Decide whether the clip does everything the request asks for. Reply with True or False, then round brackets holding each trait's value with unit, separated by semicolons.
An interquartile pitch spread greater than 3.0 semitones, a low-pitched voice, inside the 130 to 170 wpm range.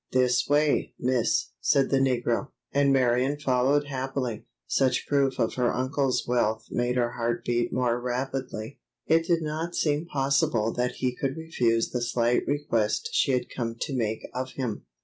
False (2.6 semitones; 130 Hz; 165 wpm)